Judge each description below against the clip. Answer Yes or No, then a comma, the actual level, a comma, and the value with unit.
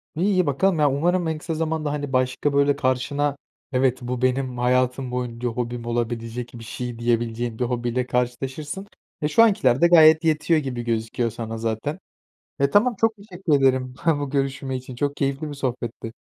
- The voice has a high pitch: No, low, 130 Hz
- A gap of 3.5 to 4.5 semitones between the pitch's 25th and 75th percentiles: Yes, average, 3.8 semitones